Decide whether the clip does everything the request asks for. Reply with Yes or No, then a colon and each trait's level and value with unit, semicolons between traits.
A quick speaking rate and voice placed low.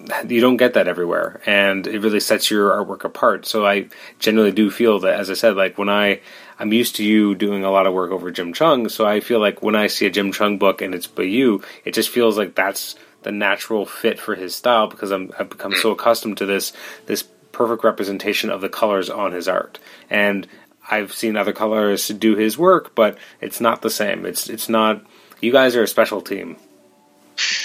Yes: fast, 220 wpm; low, 105 Hz